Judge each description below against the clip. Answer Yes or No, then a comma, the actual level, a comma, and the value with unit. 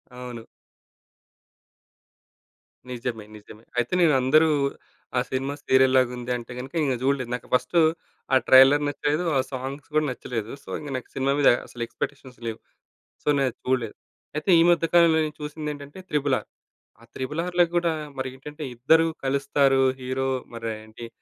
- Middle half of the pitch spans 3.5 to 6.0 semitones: No, average, 3.0 semitones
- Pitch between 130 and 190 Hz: Yes, low, 135 Hz